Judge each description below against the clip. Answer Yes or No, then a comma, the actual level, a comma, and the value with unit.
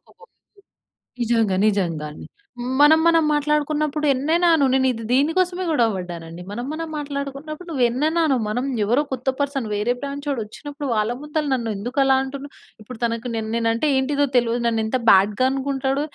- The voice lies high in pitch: Yes, very high, 265 Hz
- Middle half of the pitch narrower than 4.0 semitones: No, average, 4.4 semitones